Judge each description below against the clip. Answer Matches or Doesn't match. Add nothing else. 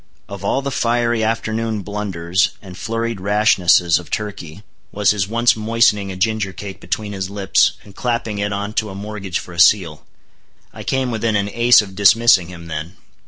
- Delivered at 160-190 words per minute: Matches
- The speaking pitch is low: Matches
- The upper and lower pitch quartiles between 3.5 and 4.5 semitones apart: Doesn't match